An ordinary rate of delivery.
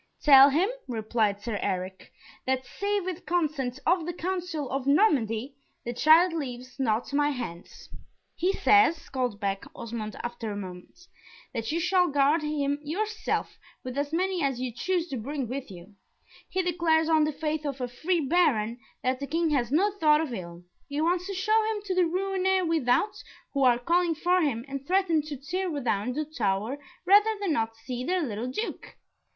Yes: average, 180 wpm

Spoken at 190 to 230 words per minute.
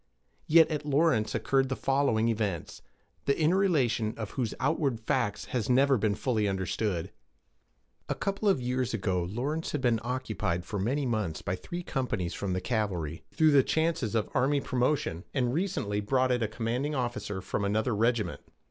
No: average, 175 wpm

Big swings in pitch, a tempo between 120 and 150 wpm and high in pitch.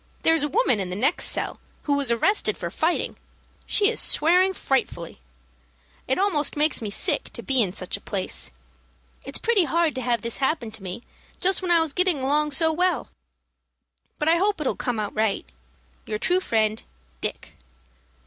No: wide, 7.6 semitones; average, 185 wpm; very high, 285 Hz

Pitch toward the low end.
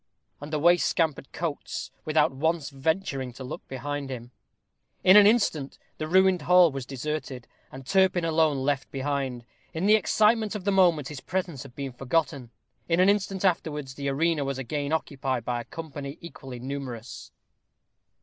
No: medium, 145 Hz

